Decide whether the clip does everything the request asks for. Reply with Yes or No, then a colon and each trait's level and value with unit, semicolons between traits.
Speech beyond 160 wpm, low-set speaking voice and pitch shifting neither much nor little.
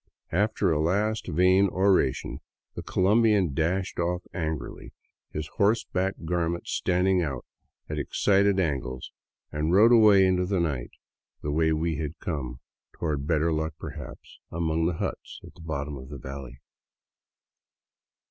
No: average, 140 wpm; very low, 85 Hz; average, 3.9 semitones